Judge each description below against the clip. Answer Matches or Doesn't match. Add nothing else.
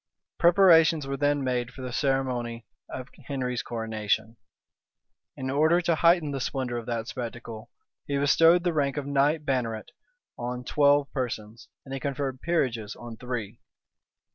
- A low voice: Matches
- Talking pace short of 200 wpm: Matches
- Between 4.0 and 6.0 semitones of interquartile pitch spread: Doesn't match